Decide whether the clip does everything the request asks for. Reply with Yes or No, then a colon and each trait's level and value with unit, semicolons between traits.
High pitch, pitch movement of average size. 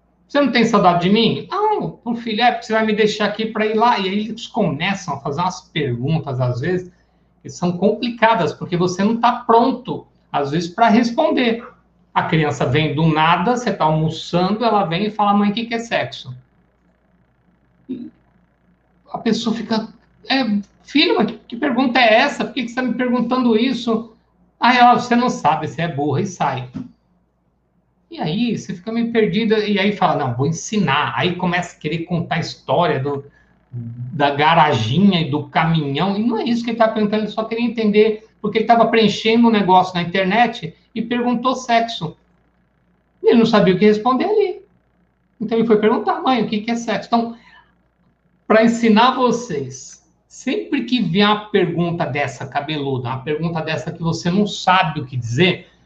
No: high, 210 Hz; wide, 6.0 semitones